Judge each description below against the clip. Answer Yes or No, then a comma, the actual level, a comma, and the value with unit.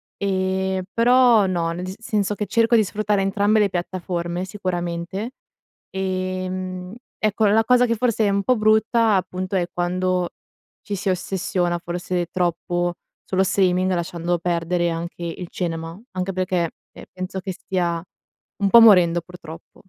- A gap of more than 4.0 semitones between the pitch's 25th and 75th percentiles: No, narrow, 2.5 semitones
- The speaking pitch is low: No, medium, 185 Hz